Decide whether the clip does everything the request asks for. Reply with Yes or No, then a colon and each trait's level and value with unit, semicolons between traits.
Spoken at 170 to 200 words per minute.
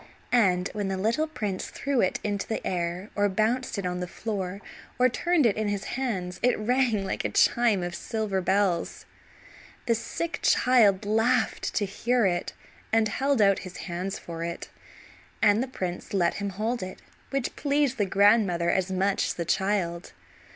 Yes: average, 175 wpm